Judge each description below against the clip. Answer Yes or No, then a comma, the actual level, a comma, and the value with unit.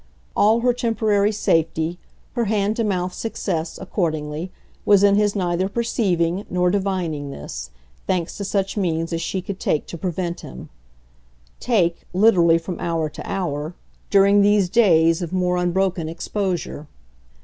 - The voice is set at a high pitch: No, medium, 180 Hz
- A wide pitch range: No, average, 3.4 semitones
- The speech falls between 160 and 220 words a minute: No, average, 145 wpm